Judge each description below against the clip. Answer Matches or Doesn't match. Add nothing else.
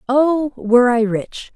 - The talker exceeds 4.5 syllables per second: Doesn't match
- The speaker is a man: Doesn't match